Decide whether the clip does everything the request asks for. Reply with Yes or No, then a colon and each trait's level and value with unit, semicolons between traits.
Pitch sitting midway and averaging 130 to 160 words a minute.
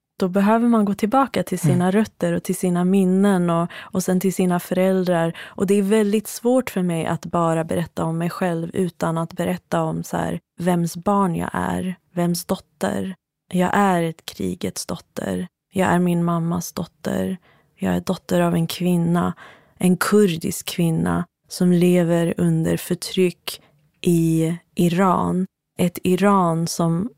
Yes: medium, 175 Hz; average, 155 wpm